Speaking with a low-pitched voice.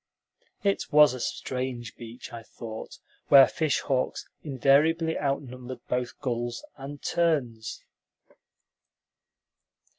Yes: low, 130 Hz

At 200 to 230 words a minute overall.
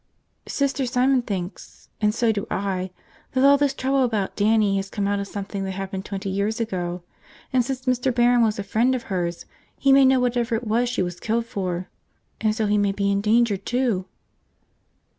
Yes: fast, 205 wpm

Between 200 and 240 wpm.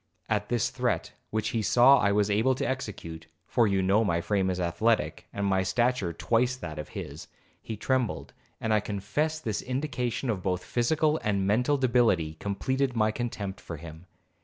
No: average, 180 wpm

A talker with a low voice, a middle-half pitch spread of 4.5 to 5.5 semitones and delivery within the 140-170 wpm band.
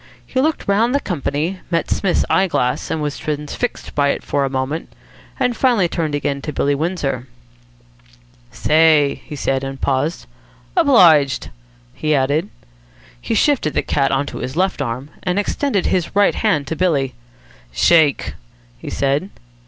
No: medium, 155 Hz; average, 5.0 semitones; average, 150 wpm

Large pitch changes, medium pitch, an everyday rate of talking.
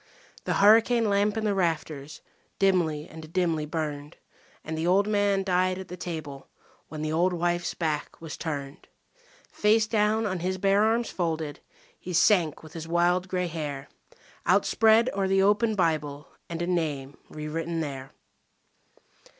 No: average, 4.1 semitones; medium, 175 Hz; average, 155 wpm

